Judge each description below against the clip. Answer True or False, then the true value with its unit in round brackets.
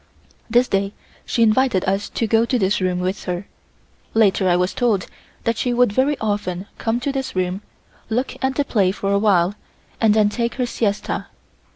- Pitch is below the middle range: False (210 Hz)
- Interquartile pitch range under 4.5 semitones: True (4.0 semitones)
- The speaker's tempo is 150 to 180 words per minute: False (190 wpm)